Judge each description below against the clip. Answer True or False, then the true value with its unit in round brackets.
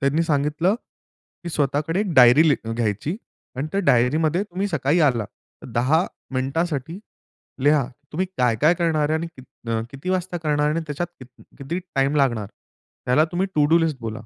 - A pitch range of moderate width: True (4.3 semitones)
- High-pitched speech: False (150 Hz)